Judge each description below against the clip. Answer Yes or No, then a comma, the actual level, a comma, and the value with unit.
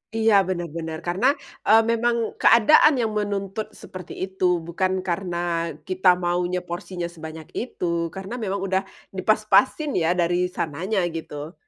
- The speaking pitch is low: No, medium, 185 Hz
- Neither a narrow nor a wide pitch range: Yes, average, 3.3 semitones